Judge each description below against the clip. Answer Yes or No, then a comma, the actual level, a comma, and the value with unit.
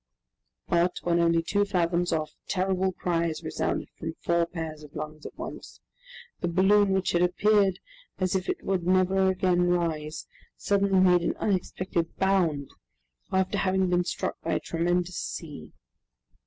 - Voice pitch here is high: No, medium, 180 Hz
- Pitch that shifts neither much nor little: No, narrow, 2.1 semitones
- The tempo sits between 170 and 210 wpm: No, average, 150 wpm